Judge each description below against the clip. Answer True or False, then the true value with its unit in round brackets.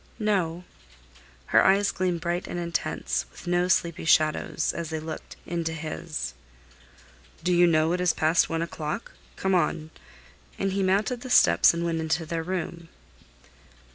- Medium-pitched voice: True (170 Hz)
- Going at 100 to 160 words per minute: True (155 wpm)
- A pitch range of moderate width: False (2.0 semitones)